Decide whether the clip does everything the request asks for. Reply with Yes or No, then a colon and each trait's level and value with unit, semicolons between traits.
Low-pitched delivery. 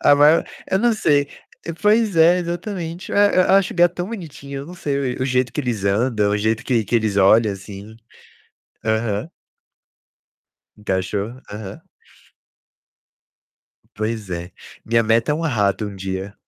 Yes: low, 120 Hz